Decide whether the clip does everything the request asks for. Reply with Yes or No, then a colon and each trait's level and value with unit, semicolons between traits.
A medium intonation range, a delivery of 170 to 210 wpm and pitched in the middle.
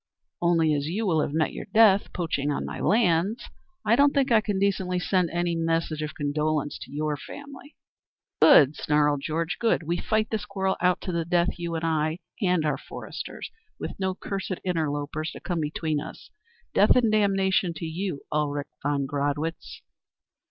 Yes: average, 4.1 semitones; average, 175 wpm; medium, 170 Hz